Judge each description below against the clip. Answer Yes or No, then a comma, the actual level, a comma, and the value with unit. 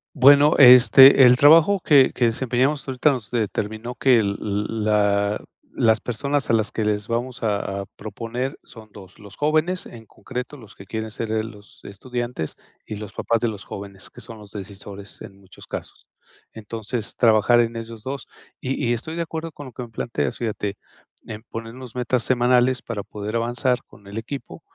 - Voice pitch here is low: Yes, low, 115 Hz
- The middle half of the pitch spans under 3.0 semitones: No, average, 3.4 semitones